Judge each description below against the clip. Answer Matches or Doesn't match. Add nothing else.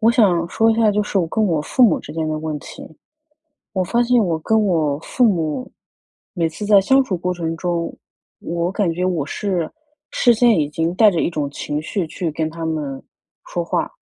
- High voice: Doesn't match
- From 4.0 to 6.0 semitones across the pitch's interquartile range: Matches